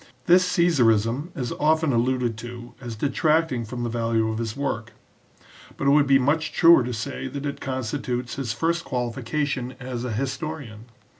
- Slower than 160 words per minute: No, average, 165 wpm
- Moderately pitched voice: No, low, 130 Hz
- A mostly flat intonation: No, average, 3.6 semitones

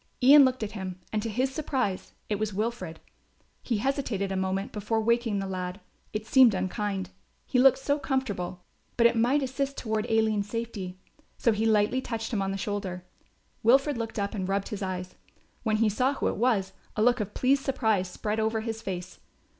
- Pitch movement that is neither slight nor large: Yes, average, 4.0 semitones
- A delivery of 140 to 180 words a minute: No, average, 195 wpm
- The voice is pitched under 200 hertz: No, high, 220 Hz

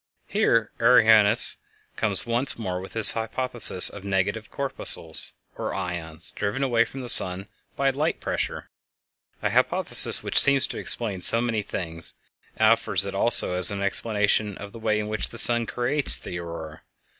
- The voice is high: No, low, 110 Hz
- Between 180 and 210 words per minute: No, average, 155 wpm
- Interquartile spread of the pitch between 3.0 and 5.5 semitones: Yes, average, 3.9 semitones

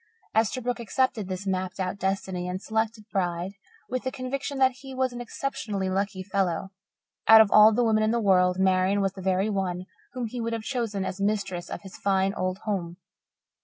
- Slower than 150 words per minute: No, average, 195 wpm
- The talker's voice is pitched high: Yes, high, 200 Hz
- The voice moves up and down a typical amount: Yes, average, 3.5 semitones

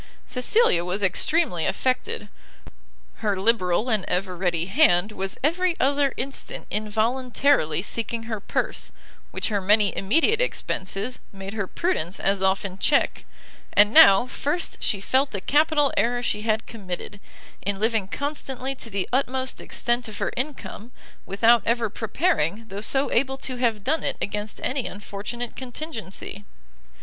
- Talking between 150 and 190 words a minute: No, average, 140 wpm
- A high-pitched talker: Yes, high, 225 Hz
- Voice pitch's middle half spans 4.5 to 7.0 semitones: Yes, average, 5.1 semitones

